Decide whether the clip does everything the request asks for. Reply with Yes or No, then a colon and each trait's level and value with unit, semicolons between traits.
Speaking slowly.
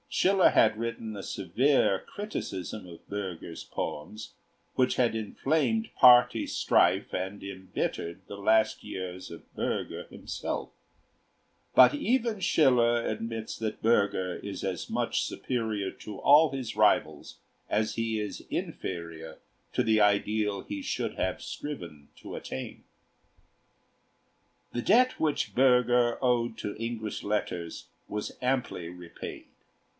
Yes: slow, 120 wpm